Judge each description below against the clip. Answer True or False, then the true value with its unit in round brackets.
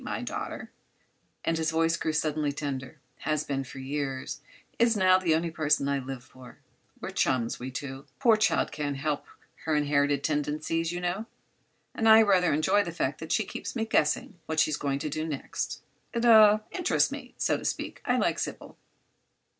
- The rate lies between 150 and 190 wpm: True (175 wpm)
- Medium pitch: True (155 Hz)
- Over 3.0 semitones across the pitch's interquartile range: True (4.1 semitones)